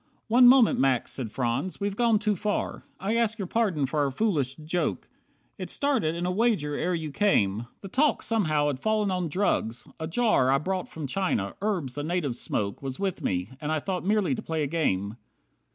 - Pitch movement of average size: No, wide, 7.1 semitones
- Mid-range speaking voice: Yes, medium, 170 Hz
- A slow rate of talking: No, average, 200 wpm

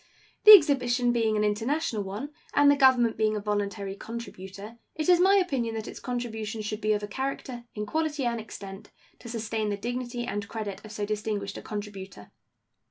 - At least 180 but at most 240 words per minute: Yes, average, 185 wpm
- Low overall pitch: No, high, 220 Hz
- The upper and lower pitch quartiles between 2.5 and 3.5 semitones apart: Yes, average, 3.1 semitones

